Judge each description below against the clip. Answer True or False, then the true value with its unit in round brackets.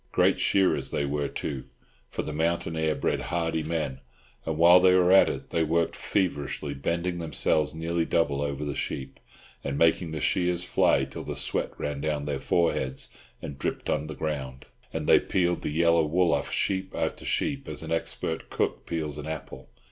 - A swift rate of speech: False (185 wpm)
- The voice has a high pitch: False (80 Hz)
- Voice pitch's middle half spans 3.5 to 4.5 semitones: False (2.7 semitones)